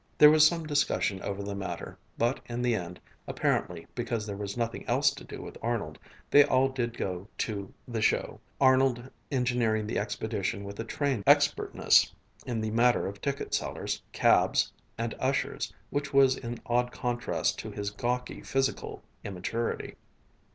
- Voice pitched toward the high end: No, low, 120 Hz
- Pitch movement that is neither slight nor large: Yes, average, 4.0 semitones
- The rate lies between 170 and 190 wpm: No, average, 160 wpm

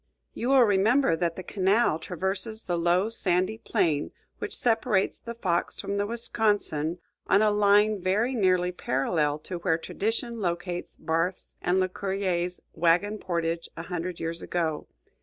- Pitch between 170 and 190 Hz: Yes, medium, 185 Hz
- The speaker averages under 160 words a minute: Yes, average, 145 wpm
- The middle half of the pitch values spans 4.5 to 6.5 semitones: No, average, 3.6 semitones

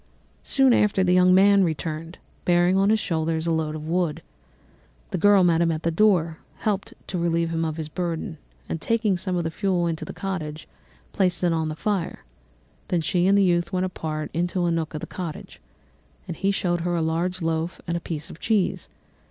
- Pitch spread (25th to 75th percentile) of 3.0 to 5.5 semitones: No, narrow, 2.5 semitones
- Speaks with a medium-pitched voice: Yes, medium, 175 Hz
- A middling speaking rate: No, fast, 210 wpm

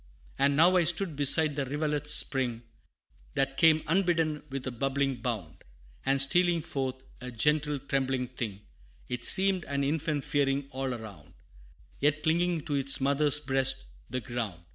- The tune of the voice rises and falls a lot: No, average, 2.9 semitones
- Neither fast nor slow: Yes, average, 150 wpm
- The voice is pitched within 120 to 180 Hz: Yes, medium, 140 Hz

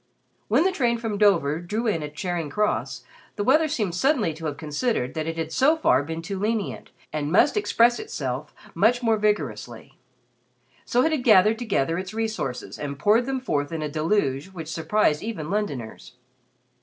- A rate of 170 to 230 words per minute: Yes, average, 180 wpm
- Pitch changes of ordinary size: No, wide, 6.8 semitones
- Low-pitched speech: No, high, 195 Hz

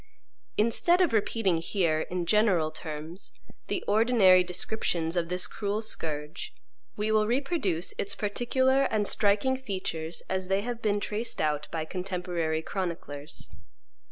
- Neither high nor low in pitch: No, high, 195 Hz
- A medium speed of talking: No, slow, 130 wpm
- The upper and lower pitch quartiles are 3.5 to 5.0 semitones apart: Yes, average, 4.7 semitones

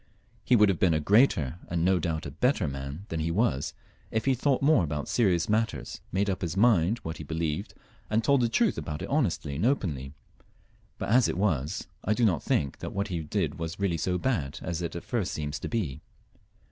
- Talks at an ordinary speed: No, fast, 225 wpm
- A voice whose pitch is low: Yes, very low, 90 Hz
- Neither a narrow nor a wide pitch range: No, wide, 6.0 semitones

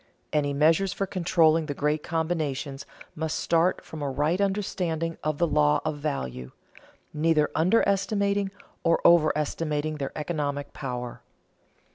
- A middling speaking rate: No, slow, 125 wpm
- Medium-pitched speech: Yes, medium, 155 Hz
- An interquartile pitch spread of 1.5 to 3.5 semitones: Yes, average, 2.9 semitones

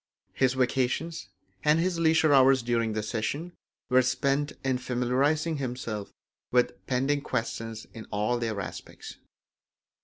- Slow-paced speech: Yes, slow, 125 wpm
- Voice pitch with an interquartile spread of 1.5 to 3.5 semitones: No, average, 3.9 semitones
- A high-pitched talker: No, low, 130 Hz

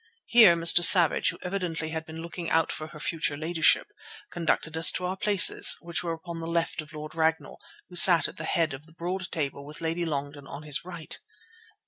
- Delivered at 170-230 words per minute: Yes, fast, 205 wpm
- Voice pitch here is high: No, medium, 165 Hz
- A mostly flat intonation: Yes, narrow, 1.8 semitones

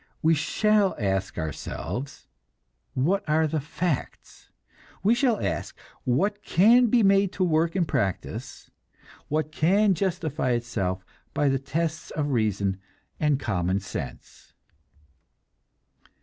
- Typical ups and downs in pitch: No, wide, 8.2 semitones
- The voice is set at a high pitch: No, medium, 155 Hz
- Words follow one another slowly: Yes, slow, 115 wpm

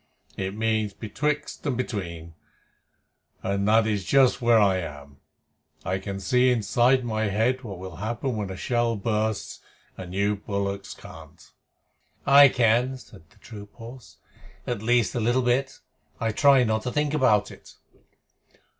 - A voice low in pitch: Yes, low, 110 Hz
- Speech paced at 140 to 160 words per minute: Yes, average, 150 wpm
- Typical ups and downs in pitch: Yes, average, 3.9 semitones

